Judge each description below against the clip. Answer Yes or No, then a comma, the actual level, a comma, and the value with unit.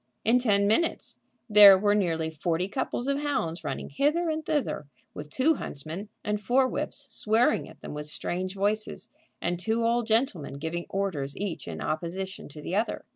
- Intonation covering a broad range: Yes, wide, 5.9 semitones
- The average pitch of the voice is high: Yes, high, 200 Hz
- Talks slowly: No, average, 175 wpm